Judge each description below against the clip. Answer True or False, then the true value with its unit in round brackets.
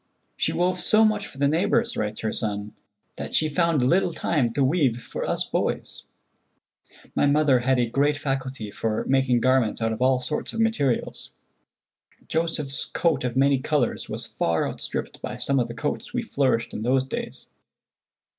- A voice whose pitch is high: False (135 Hz)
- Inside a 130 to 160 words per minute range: False (175 wpm)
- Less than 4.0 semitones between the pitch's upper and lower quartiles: False (4.4 semitones)